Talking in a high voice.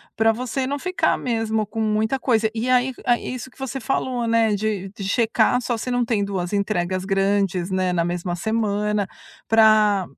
Yes: high, 220 Hz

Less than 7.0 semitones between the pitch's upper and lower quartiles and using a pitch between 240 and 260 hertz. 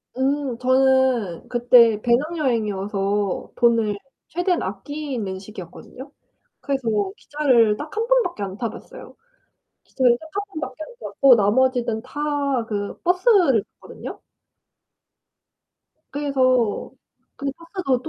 Yes: average, 5.2 semitones; very high, 255 Hz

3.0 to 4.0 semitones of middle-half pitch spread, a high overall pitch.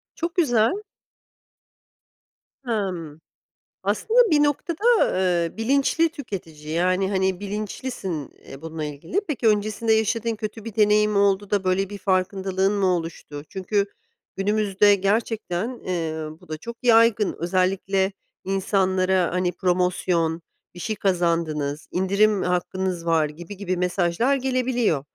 Yes: average, 3.6 semitones; high, 195 Hz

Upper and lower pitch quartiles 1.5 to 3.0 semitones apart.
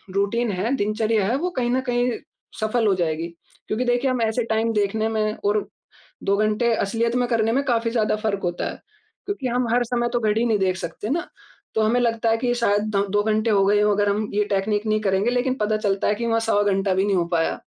Yes: average, 2.7 semitones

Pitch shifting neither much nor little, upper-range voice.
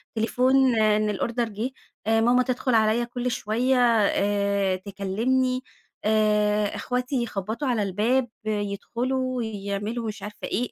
Yes: average, 3.1 semitones; high, 225 Hz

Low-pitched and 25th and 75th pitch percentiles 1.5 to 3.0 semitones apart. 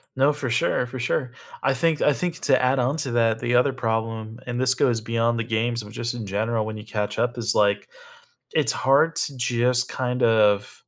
Yes: low, 120 Hz; narrow, 2.4 semitones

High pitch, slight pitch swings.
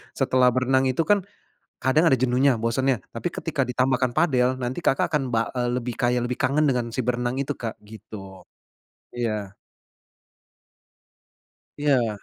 No: low, 125 Hz; narrow, 1.9 semitones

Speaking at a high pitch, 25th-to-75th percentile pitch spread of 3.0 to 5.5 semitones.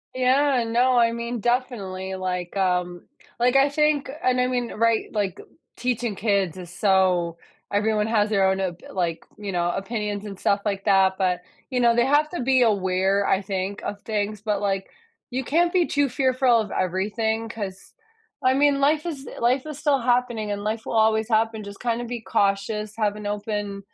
Yes: high, 215 Hz; average, 4.0 semitones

